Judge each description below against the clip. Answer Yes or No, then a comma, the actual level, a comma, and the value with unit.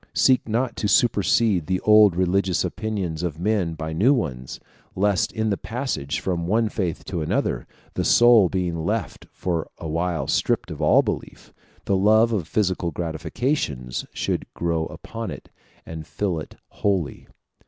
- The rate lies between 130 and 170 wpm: Yes, average, 155 wpm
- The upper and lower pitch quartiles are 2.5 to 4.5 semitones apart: No, average, 4.9 semitones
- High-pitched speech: No, very low, 95 Hz